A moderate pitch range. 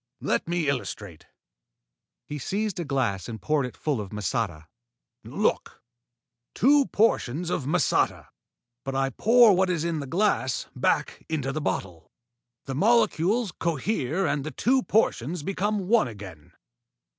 No: wide, 7.6 semitones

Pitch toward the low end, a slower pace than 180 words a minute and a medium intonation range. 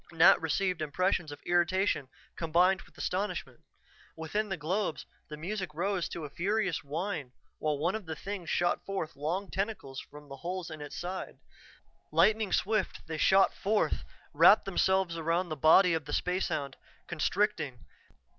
No: medium, 175 Hz; average, 155 wpm; average, 3.8 semitones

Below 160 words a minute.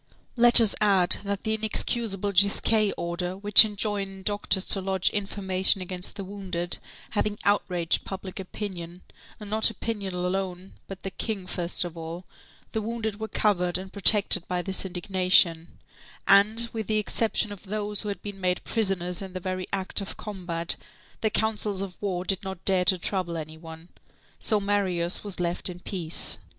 No: average, 165 wpm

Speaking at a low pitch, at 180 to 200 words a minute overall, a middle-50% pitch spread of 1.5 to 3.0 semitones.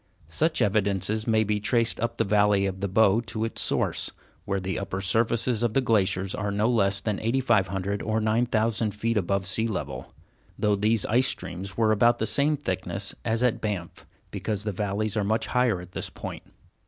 Yes: low, 105 Hz; average, 190 wpm; average, 2.7 semitones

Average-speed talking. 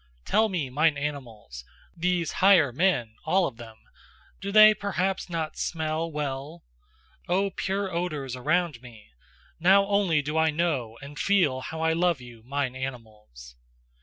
Yes: average, 145 wpm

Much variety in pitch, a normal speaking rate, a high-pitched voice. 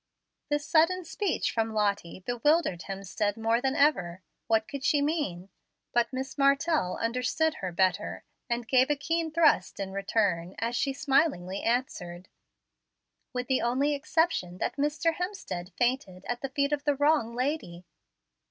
Yes: wide, 6.8 semitones; average, 150 wpm; very high, 250 Hz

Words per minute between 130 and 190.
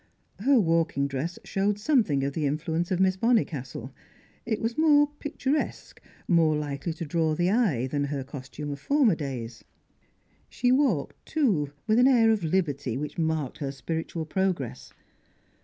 Yes: average, 155 wpm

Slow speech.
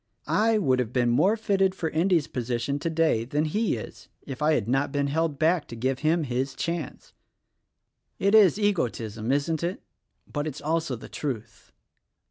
No: average, 175 wpm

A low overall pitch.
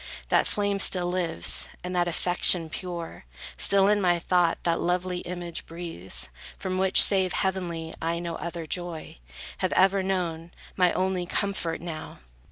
No: medium, 175 Hz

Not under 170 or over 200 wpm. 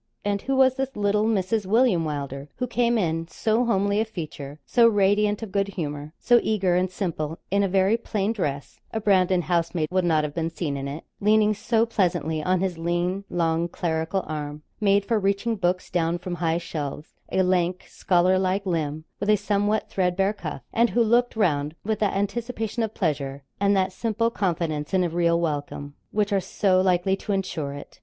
Yes: average, 190 wpm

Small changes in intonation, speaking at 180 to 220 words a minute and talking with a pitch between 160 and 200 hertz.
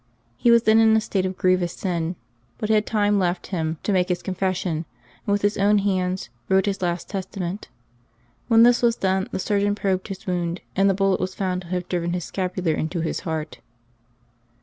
Yes: narrow, 2.2 semitones; fast, 205 wpm; high, 190 Hz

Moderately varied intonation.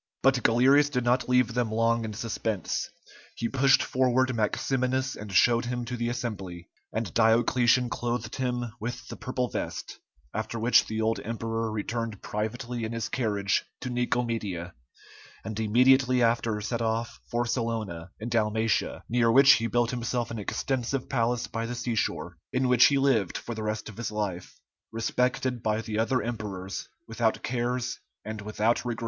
No: narrow, 2.0 semitones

